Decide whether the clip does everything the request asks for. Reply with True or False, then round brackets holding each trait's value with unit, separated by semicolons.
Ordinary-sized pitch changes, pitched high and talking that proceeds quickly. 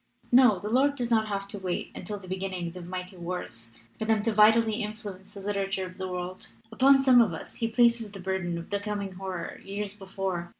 True (3.0 semitones; 200 Hz; 220 wpm)